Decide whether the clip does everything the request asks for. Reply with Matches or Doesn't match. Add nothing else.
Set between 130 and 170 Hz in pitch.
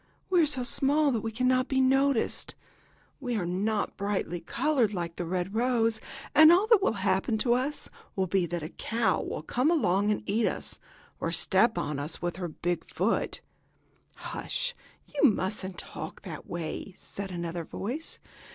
Doesn't match